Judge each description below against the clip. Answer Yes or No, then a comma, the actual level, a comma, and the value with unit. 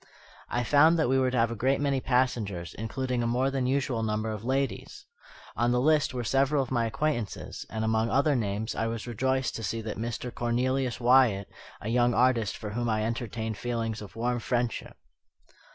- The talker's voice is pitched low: Yes, low, 120 Hz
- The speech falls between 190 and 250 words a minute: Yes, average, 200 wpm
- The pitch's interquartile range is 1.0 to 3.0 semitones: Yes, average, 2.7 semitones